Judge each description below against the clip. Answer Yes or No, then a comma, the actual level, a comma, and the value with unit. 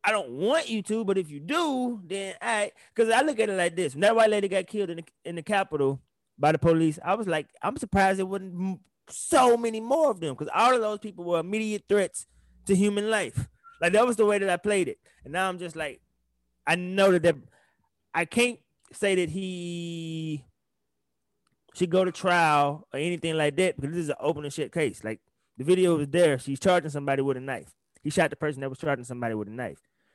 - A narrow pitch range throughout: No, average, 5.3 semitones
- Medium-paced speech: No, fast, 230 wpm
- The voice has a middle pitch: Yes, medium, 180 Hz